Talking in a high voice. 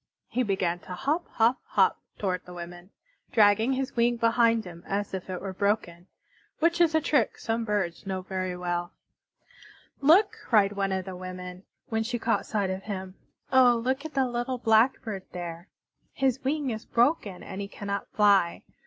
Yes: high, 210 Hz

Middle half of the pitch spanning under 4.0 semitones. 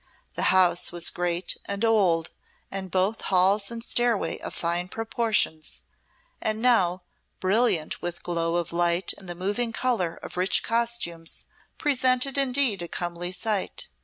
No: average, 4.8 semitones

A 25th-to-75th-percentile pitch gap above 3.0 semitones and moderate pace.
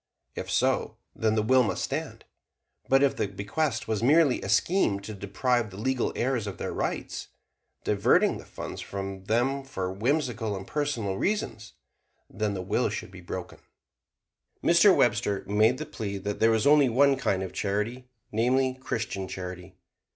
Yes: average, 4.7 semitones; average, 165 wpm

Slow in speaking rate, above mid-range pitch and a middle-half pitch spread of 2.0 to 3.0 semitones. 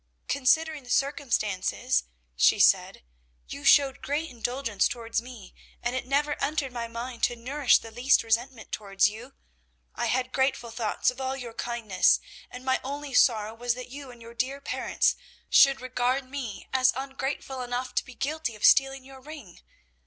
No: average, 165 wpm; very high, 255 Hz; average, 2.7 semitones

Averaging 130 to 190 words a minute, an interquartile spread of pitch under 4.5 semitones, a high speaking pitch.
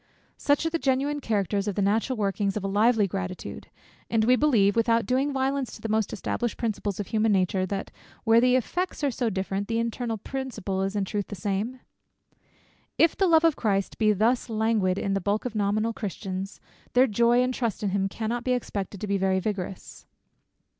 No: average, 200 wpm; average, 3.9 semitones; high, 215 Hz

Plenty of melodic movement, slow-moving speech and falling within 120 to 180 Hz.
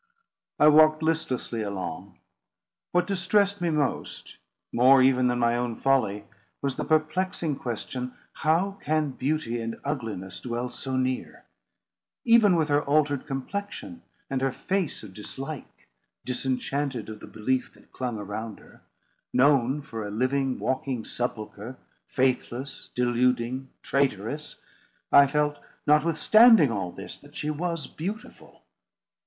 No: average, 4.2 semitones; slow, 125 wpm; low, 135 Hz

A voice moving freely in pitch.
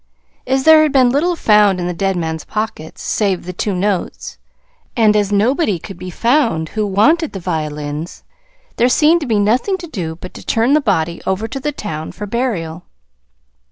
Yes: wide, 6.5 semitones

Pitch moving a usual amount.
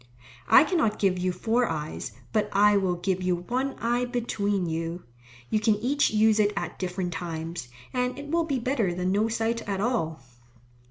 Yes: average, 5.0 semitones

